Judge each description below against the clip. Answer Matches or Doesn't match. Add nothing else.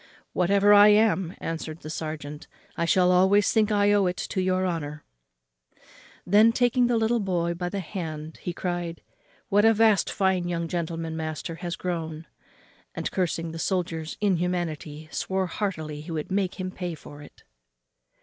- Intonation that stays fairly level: Doesn't match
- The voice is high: Doesn't match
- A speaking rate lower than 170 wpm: Matches